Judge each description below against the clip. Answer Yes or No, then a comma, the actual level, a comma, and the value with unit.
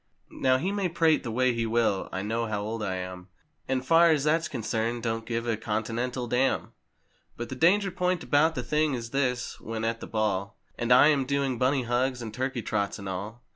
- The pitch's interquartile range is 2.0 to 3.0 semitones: No, average, 3.6 semitones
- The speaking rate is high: Yes, fast, 210 wpm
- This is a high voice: No, low, 120 Hz